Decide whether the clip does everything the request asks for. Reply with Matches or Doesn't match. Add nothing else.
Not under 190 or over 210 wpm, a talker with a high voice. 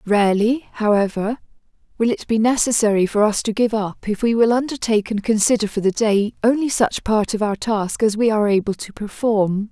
Matches